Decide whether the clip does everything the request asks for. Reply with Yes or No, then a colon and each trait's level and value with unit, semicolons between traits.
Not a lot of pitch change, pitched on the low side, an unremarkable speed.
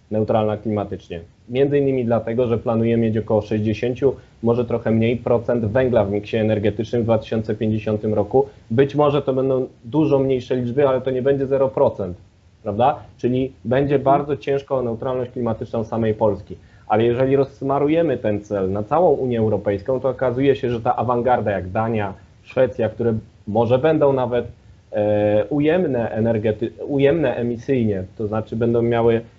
No: average, 3.4 semitones; low, 115 Hz; average, 150 wpm